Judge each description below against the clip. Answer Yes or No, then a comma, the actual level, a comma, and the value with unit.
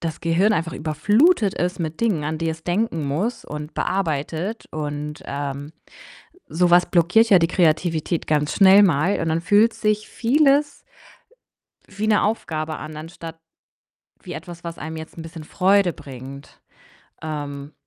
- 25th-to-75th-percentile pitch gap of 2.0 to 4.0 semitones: No, average, 4.4 semitones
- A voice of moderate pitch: Yes, medium, 165 Hz